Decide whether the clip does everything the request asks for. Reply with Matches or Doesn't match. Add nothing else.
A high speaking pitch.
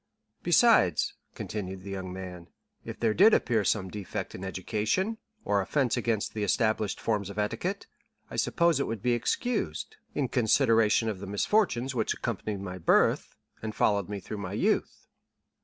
Doesn't match